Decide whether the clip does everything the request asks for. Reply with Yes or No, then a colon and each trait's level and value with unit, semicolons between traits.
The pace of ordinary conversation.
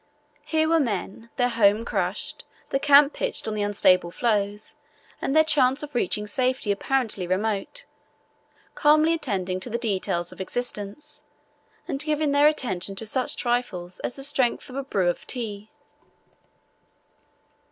Yes: average, 145 wpm